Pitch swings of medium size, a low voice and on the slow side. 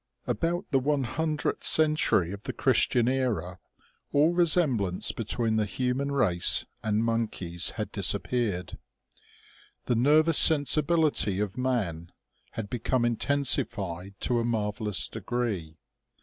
No: wide, 5.9 semitones; low, 120 Hz; slow, 120 wpm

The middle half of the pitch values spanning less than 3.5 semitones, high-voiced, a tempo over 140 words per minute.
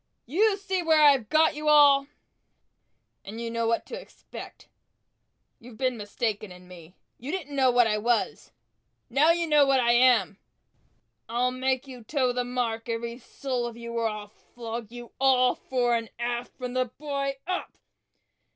Yes: average, 3.1 semitones; high, 245 Hz; average, 170 wpm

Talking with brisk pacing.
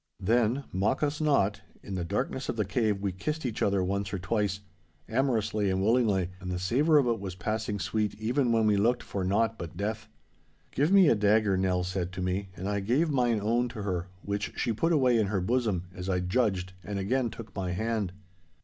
Yes: fast, 210 wpm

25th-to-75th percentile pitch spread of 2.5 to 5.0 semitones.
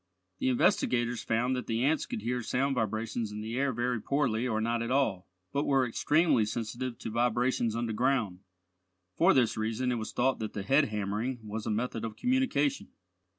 Yes: average, 2.9 semitones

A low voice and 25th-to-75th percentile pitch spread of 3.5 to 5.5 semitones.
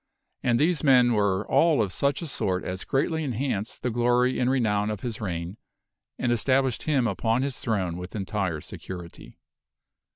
Yes: low, 115 Hz; average, 5.1 semitones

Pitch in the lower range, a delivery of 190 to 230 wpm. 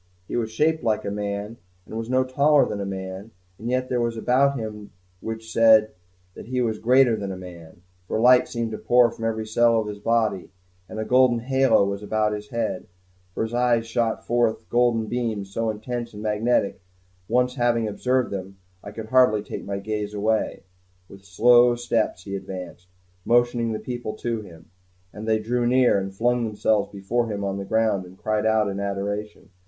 Yes: low, 110 Hz; average, 200 wpm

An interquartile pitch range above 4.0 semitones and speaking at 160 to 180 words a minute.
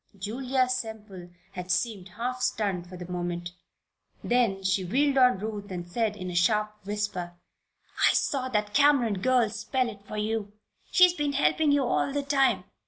Yes: average, 5.1 semitones; average, 170 wpm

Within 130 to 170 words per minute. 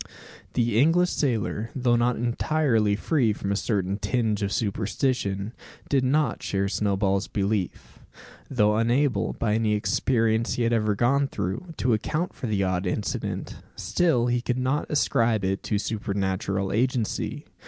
Yes: average, 145 wpm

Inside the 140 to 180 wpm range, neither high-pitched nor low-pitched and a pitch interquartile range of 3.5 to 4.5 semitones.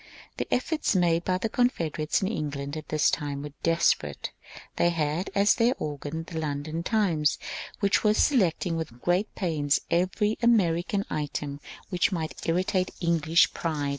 Yes: average, 160 wpm; medium, 165 Hz; average, 3.9 semitones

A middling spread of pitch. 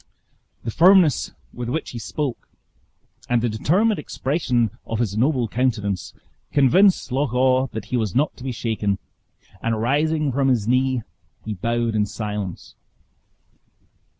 Yes: average, 3.8 semitones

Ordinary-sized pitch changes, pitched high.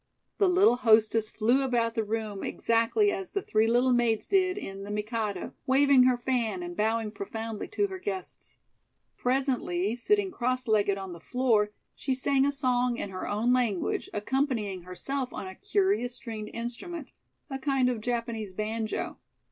Yes: average, 3.9 semitones; high, 240 Hz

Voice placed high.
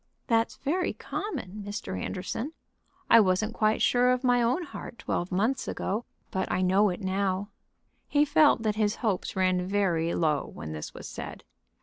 Yes: high, 205 Hz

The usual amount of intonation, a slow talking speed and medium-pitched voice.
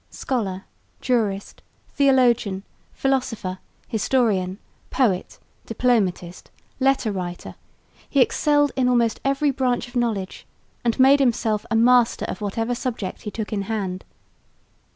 No: average, 4.3 semitones; slow, 115 wpm; high, 230 Hz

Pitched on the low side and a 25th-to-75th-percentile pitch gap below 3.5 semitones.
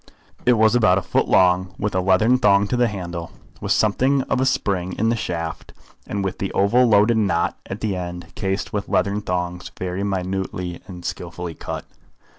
Yes: very low, 95 Hz; average, 3.0 semitones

